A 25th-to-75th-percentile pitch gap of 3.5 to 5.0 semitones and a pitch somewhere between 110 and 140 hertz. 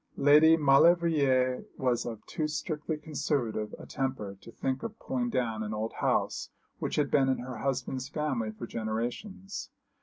Yes: average, 4.4 semitones; low, 135 Hz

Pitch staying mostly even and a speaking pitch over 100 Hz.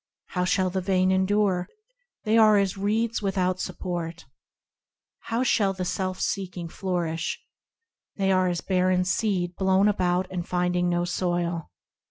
Yes: narrow, 1.6 semitones; medium, 185 Hz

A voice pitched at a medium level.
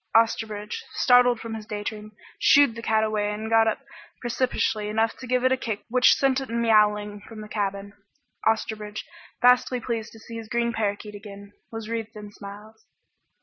No: high, 220 Hz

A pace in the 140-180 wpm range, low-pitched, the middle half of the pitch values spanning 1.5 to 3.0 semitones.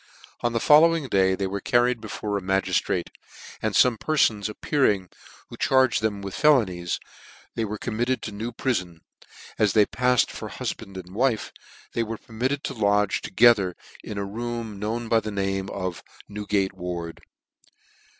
No: average, 170 wpm; low, 105 Hz; average, 3.6 semitones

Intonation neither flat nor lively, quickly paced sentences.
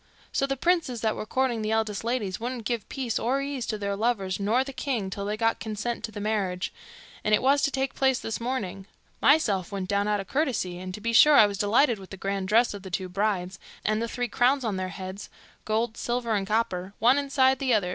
Yes: average, 4.1 semitones; fast, 235 wpm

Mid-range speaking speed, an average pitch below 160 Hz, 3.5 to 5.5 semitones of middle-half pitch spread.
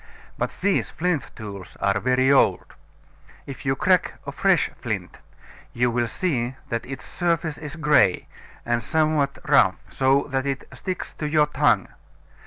Yes: average, 150 wpm; low, 135 Hz; average, 4.4 semitones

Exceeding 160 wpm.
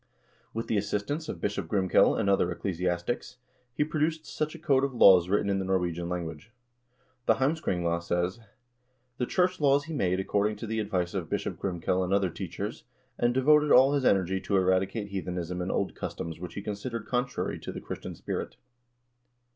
Yes: average, 180 wpm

